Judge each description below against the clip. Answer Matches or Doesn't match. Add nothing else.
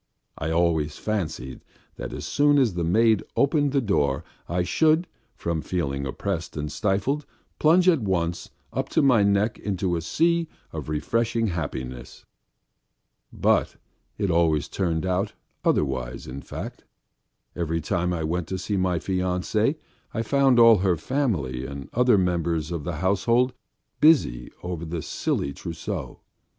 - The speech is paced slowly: Doesn't match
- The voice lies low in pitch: Matches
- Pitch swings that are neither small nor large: Doesn't match